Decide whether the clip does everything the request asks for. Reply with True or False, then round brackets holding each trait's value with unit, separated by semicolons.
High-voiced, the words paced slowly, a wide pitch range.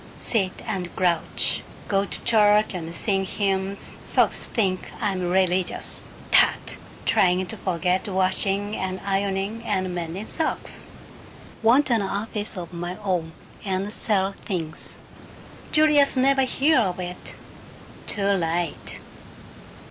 False (195 Hz; 120 wpm; 2.5 semitones)